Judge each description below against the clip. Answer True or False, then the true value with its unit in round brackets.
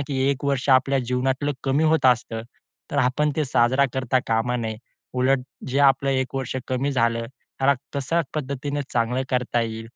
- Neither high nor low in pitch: False (130 Hz)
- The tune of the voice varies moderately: False (2.2 semitones)